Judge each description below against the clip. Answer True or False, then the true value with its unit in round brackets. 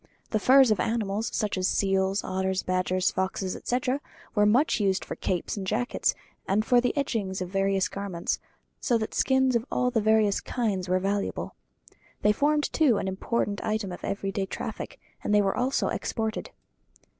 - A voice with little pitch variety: False (3.8 semitones)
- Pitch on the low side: False (205 Hz)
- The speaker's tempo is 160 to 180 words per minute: True (170 wpm)